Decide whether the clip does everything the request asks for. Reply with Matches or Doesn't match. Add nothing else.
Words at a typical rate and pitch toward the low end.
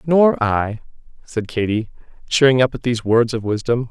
Matches